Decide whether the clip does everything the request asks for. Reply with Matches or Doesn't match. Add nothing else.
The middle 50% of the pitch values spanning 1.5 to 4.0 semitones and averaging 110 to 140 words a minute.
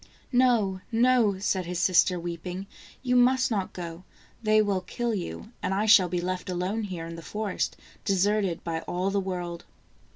Doesn't match